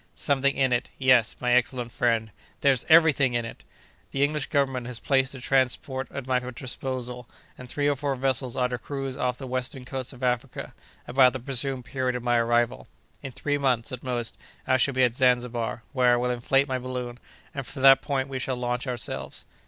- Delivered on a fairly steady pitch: Yes, narrow, 1.7 semitones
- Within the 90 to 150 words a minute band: No, average, 200 wpm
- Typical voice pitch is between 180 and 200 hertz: No, low, 130 Hz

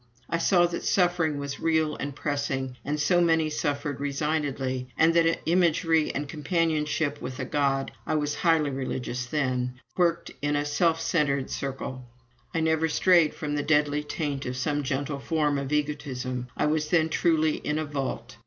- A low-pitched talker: No, medium, 150 Hz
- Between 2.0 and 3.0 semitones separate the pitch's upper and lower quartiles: Yes, narrow, 2.6 semitones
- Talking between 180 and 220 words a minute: No, average, 170 wpm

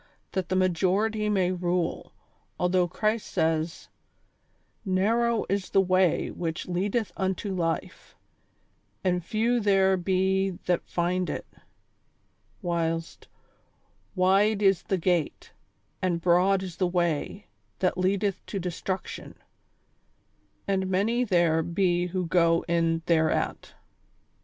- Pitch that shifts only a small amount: Yes, narrow, 2.1 semitones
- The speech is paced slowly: Yes, slow, 120 wpm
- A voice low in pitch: No, medium, 185 Hz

